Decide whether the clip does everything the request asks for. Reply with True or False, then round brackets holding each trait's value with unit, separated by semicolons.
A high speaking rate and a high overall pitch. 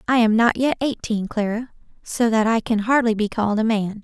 True (225 wpm; 225 Hz)